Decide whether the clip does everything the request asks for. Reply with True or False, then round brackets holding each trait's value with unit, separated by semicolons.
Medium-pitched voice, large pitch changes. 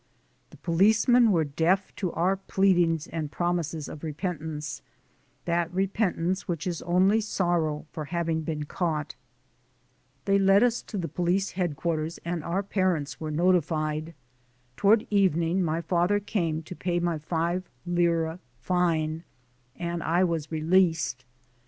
False (170 Hz; 2.7 semitones)